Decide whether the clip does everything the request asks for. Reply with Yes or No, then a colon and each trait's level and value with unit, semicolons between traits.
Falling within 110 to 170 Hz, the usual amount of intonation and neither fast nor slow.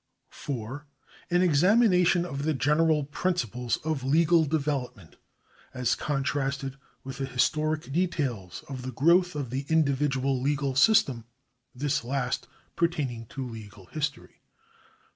No: medium, 140 Hz; average, 3.7 semitones; slow, 120 wpm